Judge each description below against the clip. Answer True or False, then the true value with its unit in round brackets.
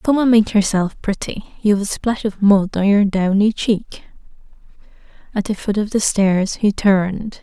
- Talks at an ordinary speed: True (180 wpm)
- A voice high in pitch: True (205 Hz)